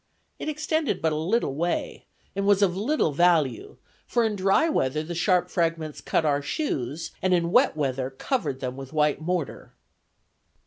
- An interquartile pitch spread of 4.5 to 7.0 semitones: Yes, wide, 5.4 semitones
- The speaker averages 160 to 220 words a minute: Yes, average, 170 wpm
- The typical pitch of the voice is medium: Yes, medium, 170 Hz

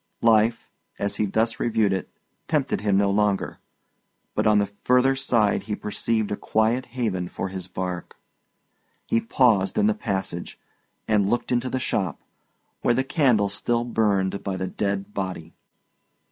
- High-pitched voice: No, low, 105 Hz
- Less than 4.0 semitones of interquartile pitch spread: Yes, average, 3.3 semitones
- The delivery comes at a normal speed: Yes, average, 155 wpm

